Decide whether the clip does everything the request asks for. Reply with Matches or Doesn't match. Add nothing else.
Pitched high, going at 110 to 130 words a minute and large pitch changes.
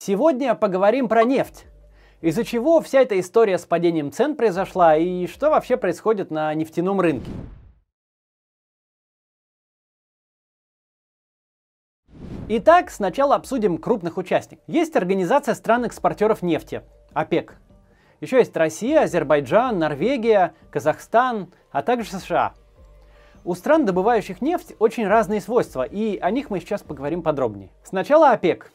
Matches